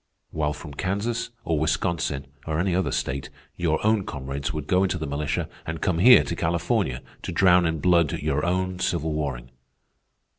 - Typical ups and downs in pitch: Yes, average, 3.7 semitones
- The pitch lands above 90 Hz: No, very low, 80 Hz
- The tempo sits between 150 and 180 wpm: Yes, average, 175 wpm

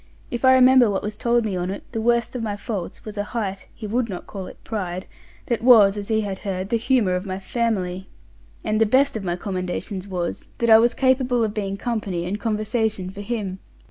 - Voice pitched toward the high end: Yes, high, 210 Hz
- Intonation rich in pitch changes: No, average, 3.6 semitones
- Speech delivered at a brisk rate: Yes, fast, 220 wpm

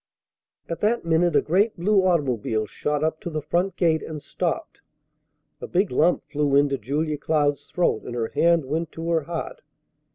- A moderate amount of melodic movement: Yes, average, 3.1 semitones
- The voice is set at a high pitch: No, medium, 160 Hz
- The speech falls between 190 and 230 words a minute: No, average, 175 wpm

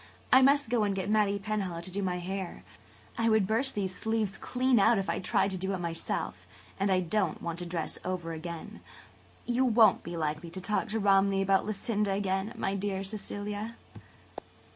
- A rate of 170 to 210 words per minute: Yes, average, 190 wpm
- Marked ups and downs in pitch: No, average, 2.8 semitones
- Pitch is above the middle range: Yes, high, 195 Hz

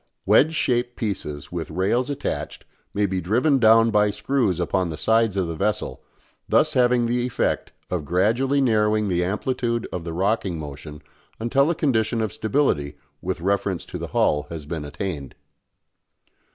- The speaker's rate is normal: Yes, average, 160 wpm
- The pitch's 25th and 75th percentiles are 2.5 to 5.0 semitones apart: No, wide, 5.6 semitones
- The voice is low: Yes, low, 105 Hz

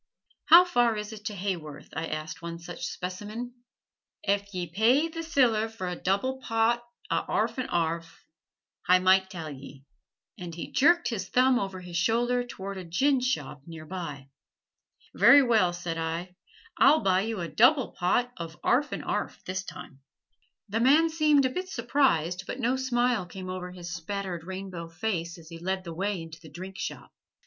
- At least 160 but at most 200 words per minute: Yes, average, 175 wpm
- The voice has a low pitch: No, high, 190 Hz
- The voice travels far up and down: Yes, wide, 6.1 semitones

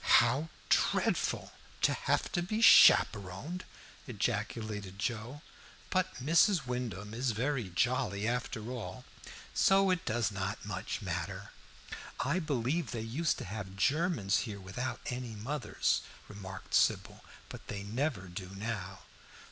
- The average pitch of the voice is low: Yes, low, 115 Hz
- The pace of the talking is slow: Yes, slow, 125 wpm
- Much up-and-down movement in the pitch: Yes, wide, 5.8 semitones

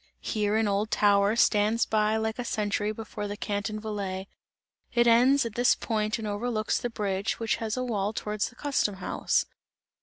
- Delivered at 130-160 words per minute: No, average, 175 wpm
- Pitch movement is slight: Yes, narrow, 1.9 semitones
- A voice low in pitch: No, high, 215 Hz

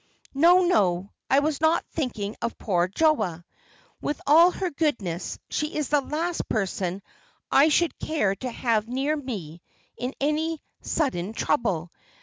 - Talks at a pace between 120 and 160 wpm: Yes, average, 140 wpm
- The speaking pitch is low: No, very high, 270 Hz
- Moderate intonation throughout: No, wide, 7.7 semitones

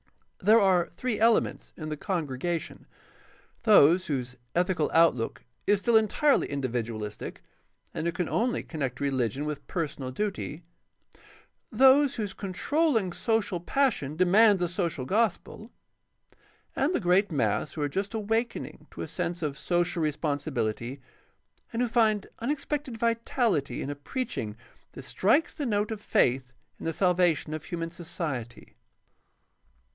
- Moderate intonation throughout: No, wide, 7.3 semitones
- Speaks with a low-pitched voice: No, medium, 175 Hz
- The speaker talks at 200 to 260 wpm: No, slow, 135 wpm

